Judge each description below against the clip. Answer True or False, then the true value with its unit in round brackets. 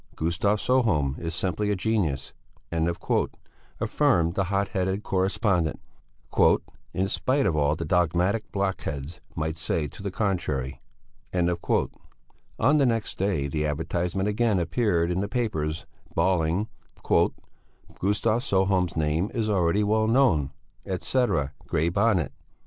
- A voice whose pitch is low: True (90 Hz)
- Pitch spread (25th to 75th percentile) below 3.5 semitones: False (4.5 semitones)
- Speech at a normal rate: False (120 wpm)